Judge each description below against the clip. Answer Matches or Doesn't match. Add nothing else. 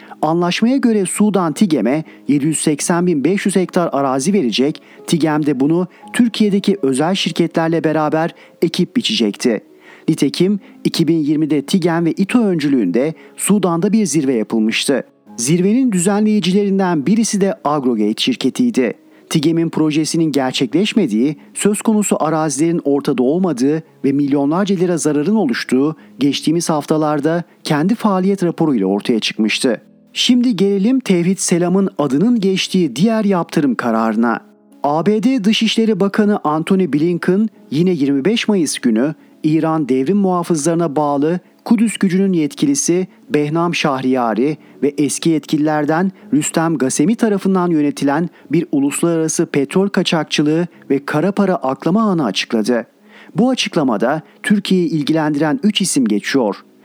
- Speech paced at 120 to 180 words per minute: Doesn't match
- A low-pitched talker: Doesn't match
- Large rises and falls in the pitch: Doesn't match